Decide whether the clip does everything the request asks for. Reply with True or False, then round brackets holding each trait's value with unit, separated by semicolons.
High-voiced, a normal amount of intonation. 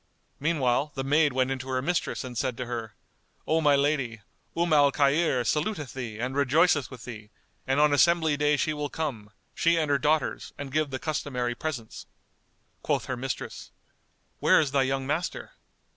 False (140 Hz; 3.0 semitones)